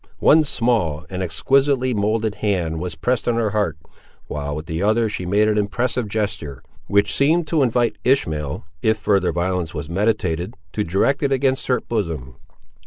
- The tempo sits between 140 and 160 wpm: No, average, 170 wpm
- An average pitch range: No, wide, 5.8 semitones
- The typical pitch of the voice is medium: No, low, 105 Hz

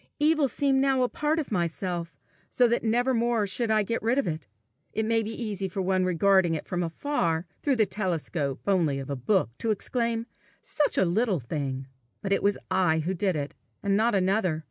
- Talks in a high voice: Yes, high, 200 Hz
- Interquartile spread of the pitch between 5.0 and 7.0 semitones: Yes, average, 5.3 semitones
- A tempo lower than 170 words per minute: No, average, 200 wpm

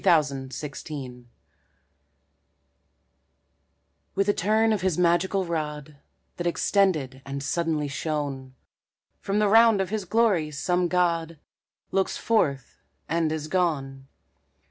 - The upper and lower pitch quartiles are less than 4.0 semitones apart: No, average, 4.9 semitones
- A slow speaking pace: Yes, slow, 110 wpm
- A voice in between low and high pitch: Yes, medium, 165 Hz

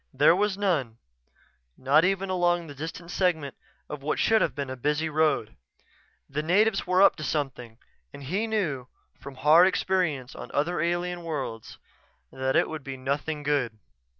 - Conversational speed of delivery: Yes, average, 165 wpm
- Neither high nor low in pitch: Yes, medium, 155 Hz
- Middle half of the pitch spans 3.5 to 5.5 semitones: Yes, average, 4.5 semitones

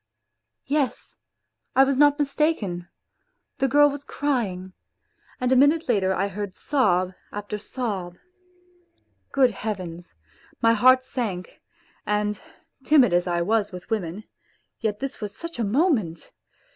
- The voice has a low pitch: No, high, 220 Hz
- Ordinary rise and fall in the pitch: No, wide, 6.2 semitones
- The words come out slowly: Yes, slow, 130 wpm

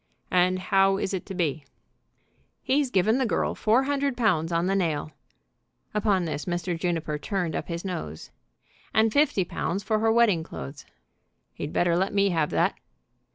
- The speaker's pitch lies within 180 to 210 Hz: Yes, medium, 185 Hz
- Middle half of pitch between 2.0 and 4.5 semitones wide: Yes, average, 4.2 semitones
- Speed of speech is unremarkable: Yes, average, 165 wpm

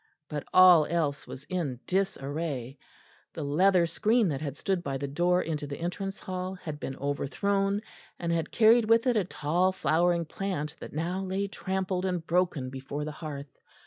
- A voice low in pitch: No, medium, 170 Hz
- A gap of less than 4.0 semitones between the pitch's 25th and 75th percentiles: No, average, 4.5 semitones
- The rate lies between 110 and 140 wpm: No, average, 175 wpm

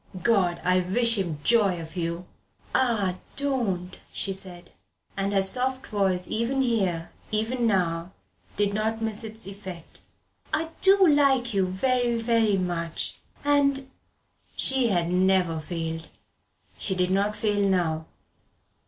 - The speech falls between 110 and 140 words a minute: Yes, slow, 135 wpm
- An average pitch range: Yes, average, 4.7 semitones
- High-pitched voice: Yes, high, 200 Hz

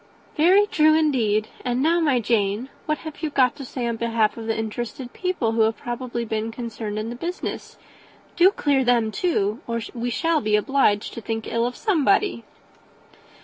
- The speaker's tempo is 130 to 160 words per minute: No, average, 190 wpm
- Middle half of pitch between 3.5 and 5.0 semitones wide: No, wide, 5.4 semitones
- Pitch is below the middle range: No, high, 240 Hz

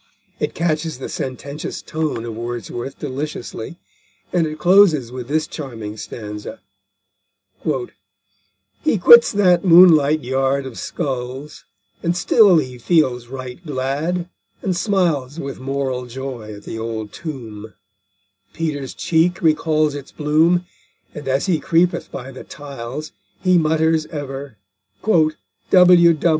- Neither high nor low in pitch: Yes, medium, 150 Hz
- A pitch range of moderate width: Yes, average, 4.5 semitones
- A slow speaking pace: Yes, slow, 120 wpm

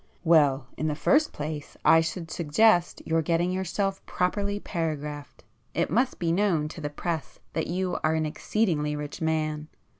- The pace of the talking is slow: No, average, 160 wpm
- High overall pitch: No, medium, 165 Hz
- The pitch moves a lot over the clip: No, average, 3.3 semitones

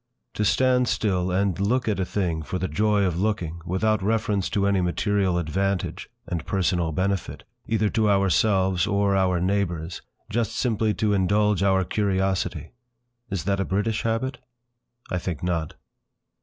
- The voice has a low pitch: Yes, low, 100 Hz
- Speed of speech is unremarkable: Yes, average, 155 wpm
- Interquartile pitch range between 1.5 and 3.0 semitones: Yes, average, 2.7 semitones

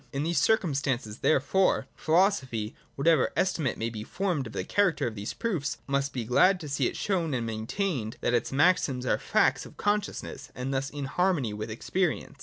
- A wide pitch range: Yes, wide, 6.9 semitones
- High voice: No, medium, 140 Hz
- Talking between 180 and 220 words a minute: Yes, fast, 205 wpm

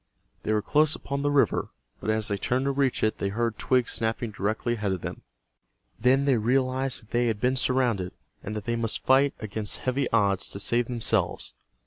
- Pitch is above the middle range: No, low, 120 Hz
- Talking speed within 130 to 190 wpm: No, average, 200 wpm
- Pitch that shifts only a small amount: No, average, 3.4 semitones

